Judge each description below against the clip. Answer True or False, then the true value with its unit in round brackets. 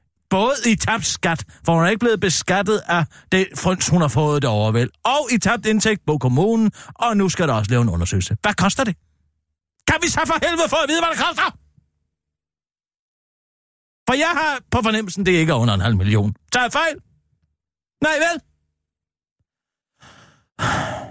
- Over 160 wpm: True (175 wpm)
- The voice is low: False (170 Hz)